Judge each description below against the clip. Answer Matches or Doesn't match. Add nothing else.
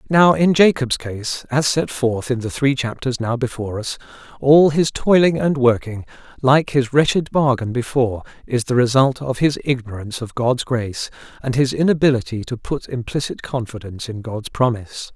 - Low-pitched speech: Matches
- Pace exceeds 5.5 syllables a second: Doesn't match